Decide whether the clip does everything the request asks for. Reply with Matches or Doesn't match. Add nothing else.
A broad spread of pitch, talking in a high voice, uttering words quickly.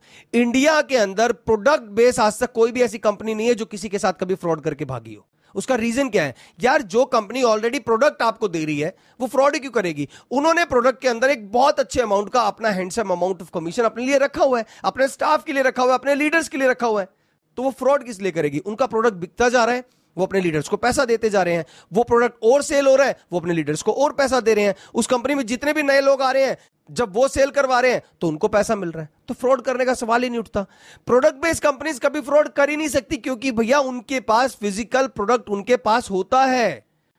Doesn't match